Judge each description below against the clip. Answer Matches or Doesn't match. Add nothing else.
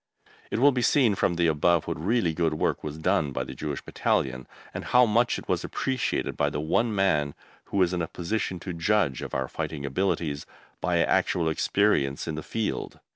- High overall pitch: Doesn't match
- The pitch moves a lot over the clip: Matches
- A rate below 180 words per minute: Doesn't match